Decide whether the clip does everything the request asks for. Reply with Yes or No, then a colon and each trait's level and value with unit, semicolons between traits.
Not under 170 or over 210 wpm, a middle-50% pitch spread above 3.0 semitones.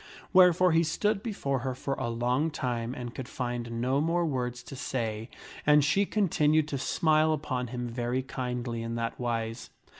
Yes: average, 175 wpm; average, 4.3 semitones